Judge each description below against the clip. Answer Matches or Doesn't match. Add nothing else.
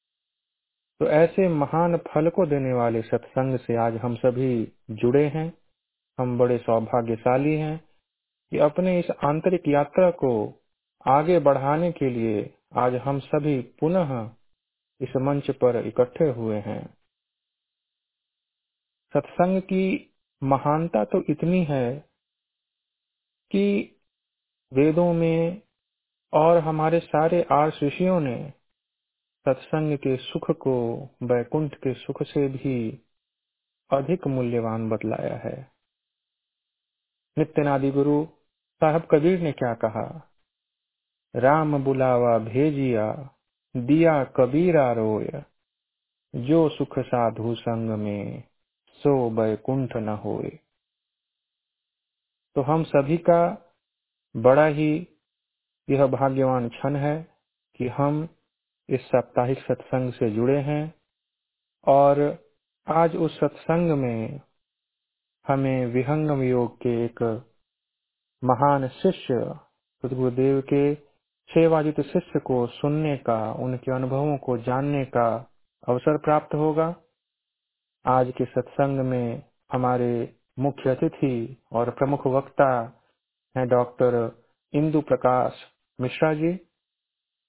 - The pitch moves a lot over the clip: Doesn't match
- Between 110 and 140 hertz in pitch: Matches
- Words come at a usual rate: Doesn't match